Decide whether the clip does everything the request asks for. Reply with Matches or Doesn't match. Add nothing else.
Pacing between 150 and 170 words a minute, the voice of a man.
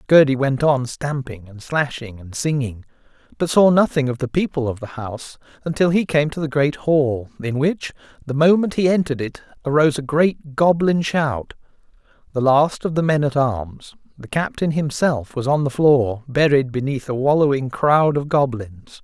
Doesn't match